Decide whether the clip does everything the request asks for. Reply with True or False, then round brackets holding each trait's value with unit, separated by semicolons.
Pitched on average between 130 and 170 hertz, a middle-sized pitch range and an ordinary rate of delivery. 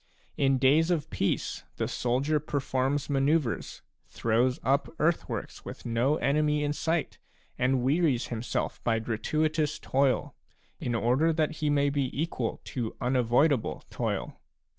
False (140 Hz; 3.5 semitones; 130 wpm)